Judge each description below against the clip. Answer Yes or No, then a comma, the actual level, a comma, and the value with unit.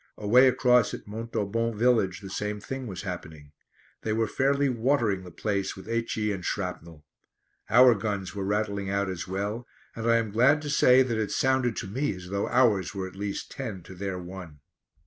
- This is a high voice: No, low, 105 Hz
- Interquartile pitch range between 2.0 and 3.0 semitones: No, average, 3.8 semitones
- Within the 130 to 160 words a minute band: No, average, 190 wpm